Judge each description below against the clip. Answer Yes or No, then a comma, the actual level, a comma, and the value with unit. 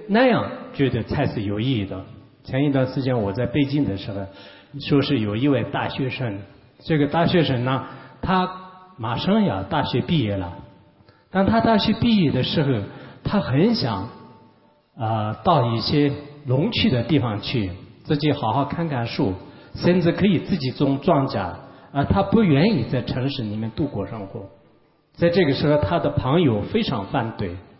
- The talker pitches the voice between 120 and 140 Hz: Yes, low, 135 Hz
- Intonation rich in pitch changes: Yes, wide, 5.9 semitones